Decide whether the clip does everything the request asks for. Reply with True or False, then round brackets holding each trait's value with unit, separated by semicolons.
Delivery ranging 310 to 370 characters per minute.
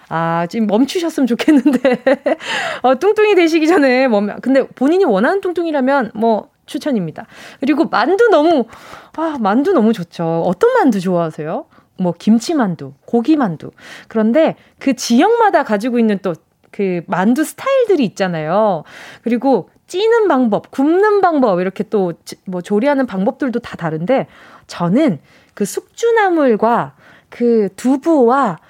False (290 characters per minute)